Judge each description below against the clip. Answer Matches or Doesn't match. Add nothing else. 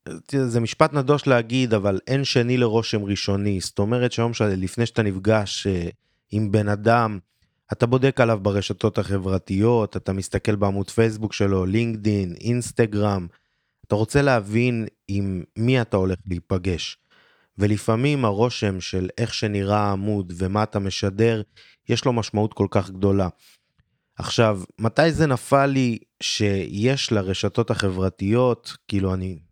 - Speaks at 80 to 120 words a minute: Doesn't match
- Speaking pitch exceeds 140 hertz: Doesn't match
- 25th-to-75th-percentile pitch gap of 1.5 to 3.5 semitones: Matches